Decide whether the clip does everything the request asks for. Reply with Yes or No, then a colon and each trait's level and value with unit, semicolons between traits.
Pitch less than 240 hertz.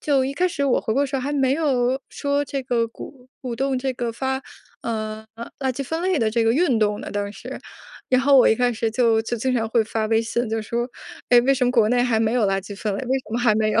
No: high, 245 Hz